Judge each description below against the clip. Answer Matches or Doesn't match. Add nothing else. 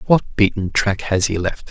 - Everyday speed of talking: Doesn't match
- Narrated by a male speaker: Matches